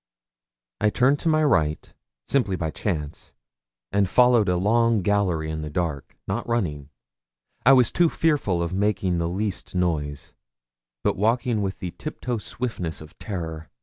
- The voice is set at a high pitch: No, very low, 95 Hz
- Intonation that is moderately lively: No, wide, 6.0 semitones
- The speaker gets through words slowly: No, average, 150 wpm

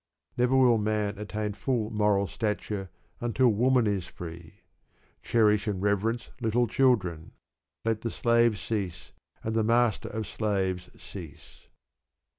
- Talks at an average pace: No, slow, 125 wpm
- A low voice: Yes, low, 110 Hz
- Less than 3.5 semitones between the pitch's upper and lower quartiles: Yes, narrow, 2.6 semitones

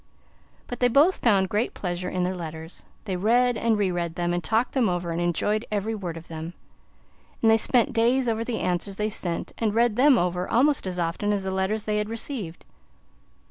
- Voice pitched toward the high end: Yes, high, 205 Hz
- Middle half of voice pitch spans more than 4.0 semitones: Yes, average, 4.5 semitones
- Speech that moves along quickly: Yes, fast, 210 wpm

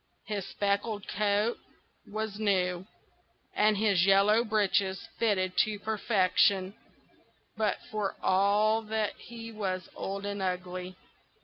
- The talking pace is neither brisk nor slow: No, slow, 110 wpm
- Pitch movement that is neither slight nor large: No, narrow, 2.2 semitones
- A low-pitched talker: No, high, 205 Hz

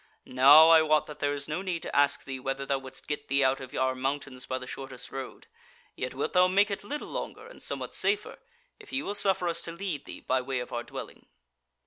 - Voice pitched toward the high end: No, medium, 145 Hz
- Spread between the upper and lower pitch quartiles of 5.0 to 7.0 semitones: Yes, average, 5.3 semitones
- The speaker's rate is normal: No, fast, 240 wpm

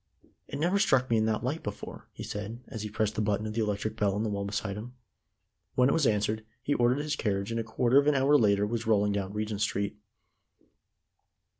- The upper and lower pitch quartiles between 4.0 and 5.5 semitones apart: No, average, 3.3 semitones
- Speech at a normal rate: No, fast, 230 wpm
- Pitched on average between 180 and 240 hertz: No, low, 110 Hz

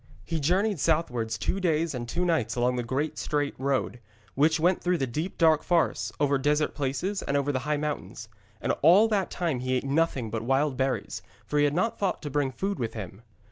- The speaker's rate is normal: No, fast, 215 wpm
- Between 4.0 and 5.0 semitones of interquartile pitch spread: Yes, average, 4.5 semitones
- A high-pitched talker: No, medium, 145 Hz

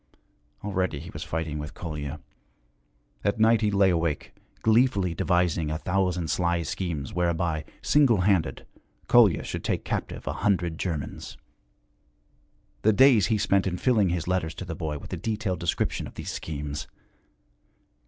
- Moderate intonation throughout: Yes, average, 4.0 semitones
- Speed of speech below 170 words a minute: Yes, average, 150 wpm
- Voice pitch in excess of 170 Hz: No, very low, 90 Hz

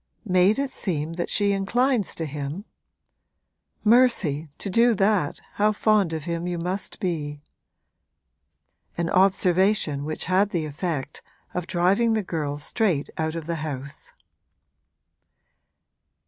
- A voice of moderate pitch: Yes, medium, 180 Hz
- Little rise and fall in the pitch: No, average, 4.6 semitones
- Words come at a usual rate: No, slow, 125 wpm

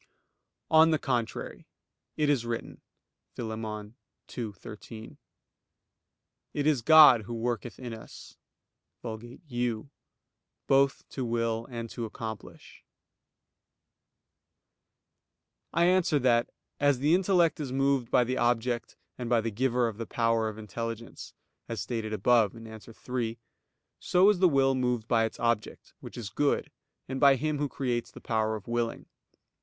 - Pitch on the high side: No, low, 120 Hz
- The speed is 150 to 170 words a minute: No, average, 140 wpm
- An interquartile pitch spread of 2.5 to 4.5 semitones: Yes, average, 3.1 semitones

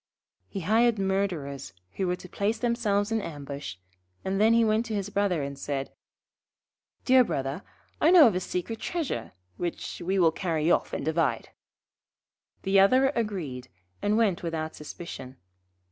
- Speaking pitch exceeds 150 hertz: Yes, high, 190 Hz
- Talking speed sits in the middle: Yes, average, 155 wpm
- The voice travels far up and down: Yes, wide, 6.0 semitones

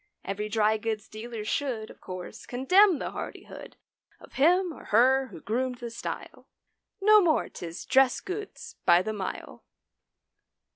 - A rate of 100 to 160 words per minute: Yes, average, 140 wpm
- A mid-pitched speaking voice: No, high, 240 Hz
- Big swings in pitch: Yes, wide, 6.3 semitones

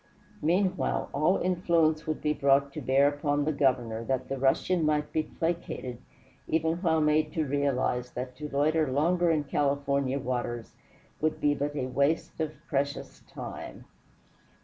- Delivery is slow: No, average, 150 wpm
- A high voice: No, medium, 145 Hz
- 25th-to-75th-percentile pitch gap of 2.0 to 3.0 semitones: Yes, narrow, 2.5 semitones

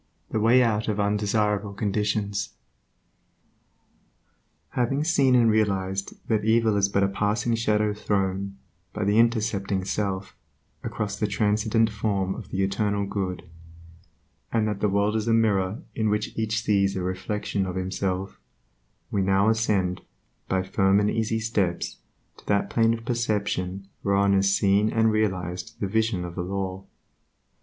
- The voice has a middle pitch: No, low, 105 Hz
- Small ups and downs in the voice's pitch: Yes, narrow, 2.1 semitones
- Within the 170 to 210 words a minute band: No, average, 150 wpm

